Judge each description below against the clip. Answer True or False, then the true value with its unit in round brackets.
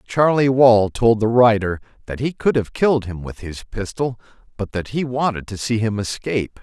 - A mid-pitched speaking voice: False (115 Hz)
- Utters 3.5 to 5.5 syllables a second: True (5.0 syllables/s)